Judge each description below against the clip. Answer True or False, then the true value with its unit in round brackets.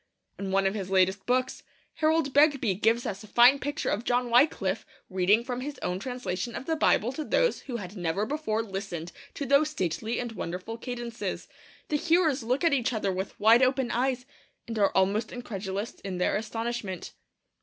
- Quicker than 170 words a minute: True (185 wpm)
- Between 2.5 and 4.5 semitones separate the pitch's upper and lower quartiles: False (4.9 semitones)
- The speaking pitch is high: True (230 Hz)